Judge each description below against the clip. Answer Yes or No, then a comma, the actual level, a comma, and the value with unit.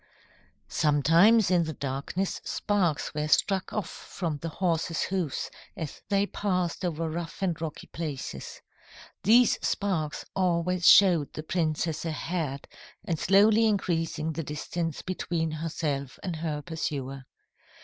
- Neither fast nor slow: No, slow, 125 wpm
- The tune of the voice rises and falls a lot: No, average, 3.2 semitones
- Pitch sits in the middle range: Yes, medium, 165 Hz